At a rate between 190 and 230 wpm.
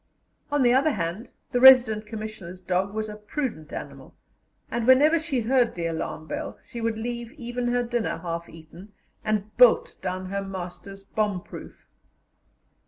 No: average, 160 wpm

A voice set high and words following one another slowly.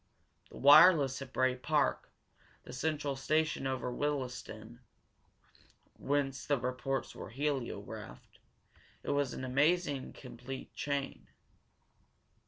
No: low, 135 Hz; slow, 100 wpm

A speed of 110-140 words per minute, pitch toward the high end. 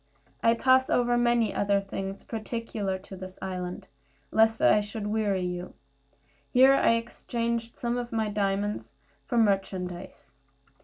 Yes: slow, 135 wpm; high, 210 Hz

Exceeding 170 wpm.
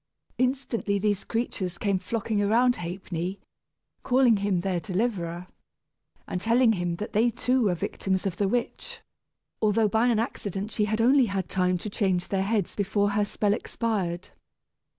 No: average, 155 wpm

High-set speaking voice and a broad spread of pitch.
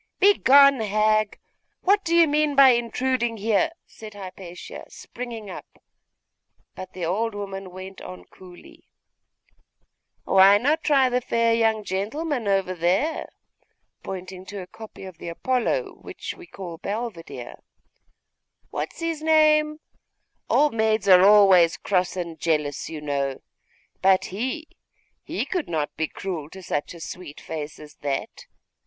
Yes: high, 205 Hz; wide, 6.1 semitones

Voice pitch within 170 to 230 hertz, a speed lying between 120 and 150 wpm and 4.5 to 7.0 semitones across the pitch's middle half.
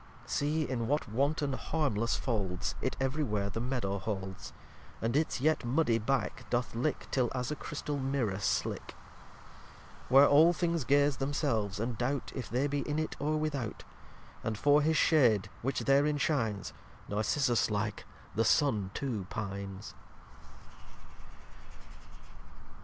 No: low, 130 Hz; average, 140 wpm; average, 5.1 semitones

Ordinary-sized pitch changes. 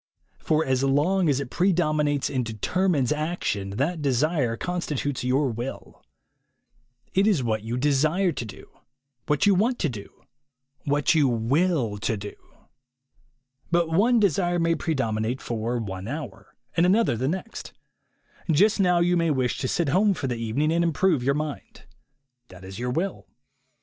No: wide, 6.0 semitones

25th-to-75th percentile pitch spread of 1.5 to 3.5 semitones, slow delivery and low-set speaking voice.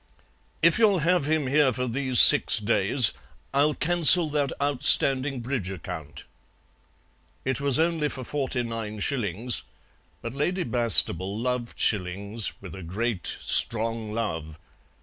No: average, 5.2 semitones; slow, 130 wpm; low, 125 Hz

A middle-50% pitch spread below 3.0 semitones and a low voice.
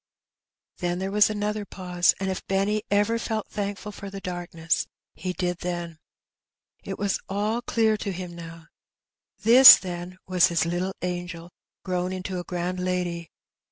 No: narrow, 2.5 semitones; medium, 185 Hz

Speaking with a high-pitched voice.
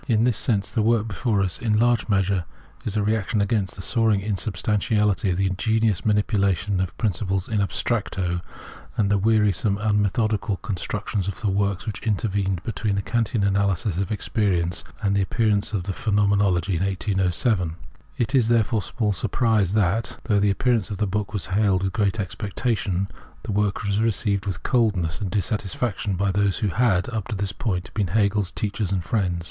No: low, 100 Hz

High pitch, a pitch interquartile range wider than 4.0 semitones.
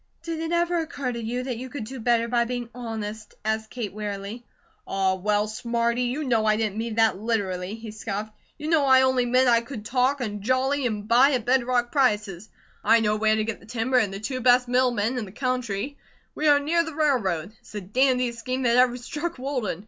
No: high, 240 Hz; average, 3.1 semitones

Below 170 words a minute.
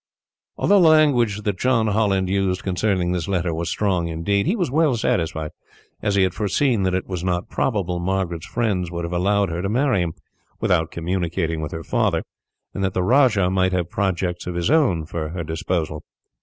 No: average, 195 wpm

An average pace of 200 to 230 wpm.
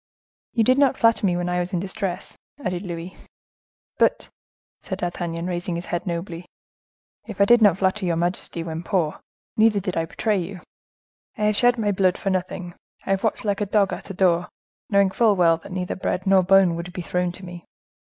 Yes: fast, 205 wpm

